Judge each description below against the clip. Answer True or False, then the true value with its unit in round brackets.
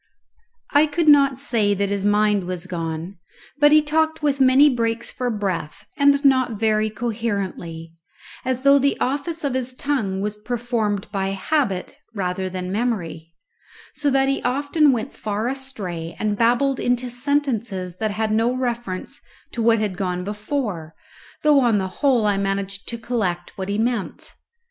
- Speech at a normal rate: True (160 wpm)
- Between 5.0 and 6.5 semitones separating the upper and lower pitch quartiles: True (5.3 semitones)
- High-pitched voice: True (225 Hz)